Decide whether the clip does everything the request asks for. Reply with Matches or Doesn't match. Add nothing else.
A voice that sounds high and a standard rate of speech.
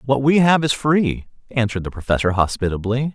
Doesn't match